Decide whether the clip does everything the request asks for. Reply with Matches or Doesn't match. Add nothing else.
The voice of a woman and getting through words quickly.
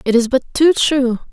Matches